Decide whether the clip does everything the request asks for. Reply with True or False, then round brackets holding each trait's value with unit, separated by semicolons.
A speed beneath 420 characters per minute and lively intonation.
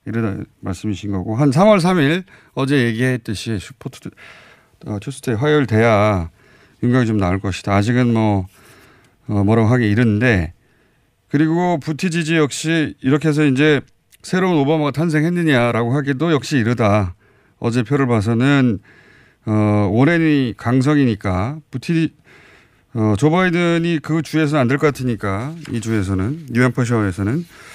True (305 characters per minute; 5.8 semitones)